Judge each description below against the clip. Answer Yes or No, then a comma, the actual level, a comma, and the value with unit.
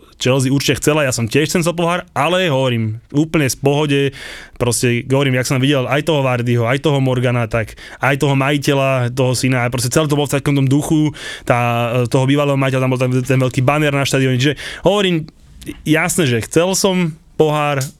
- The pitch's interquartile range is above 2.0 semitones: Yes, average, 2.8 semitones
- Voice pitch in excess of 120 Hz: Yes, medium, 140 Hz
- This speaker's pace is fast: Yes, fast, 195 wpm